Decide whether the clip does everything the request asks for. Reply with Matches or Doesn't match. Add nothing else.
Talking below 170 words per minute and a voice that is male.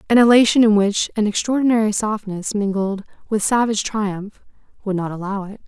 Doesn't match